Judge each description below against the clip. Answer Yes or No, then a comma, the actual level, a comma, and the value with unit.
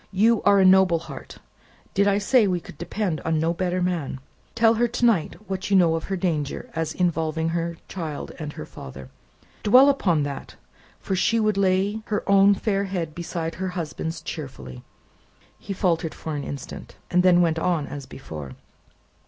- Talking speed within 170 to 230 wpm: Yes, average, 175 wpm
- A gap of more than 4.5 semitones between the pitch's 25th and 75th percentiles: No, average, 3.6 semitones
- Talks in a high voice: No, medium, 175 Hz